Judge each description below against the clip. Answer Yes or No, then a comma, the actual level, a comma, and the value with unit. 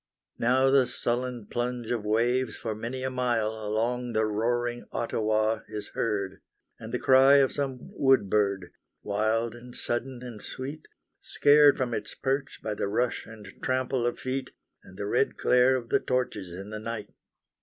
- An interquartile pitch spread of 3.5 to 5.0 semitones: No, average, 3.0 semitones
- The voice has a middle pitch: No, low, 120 Hz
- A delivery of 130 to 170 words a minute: Yes, average, 165 wpm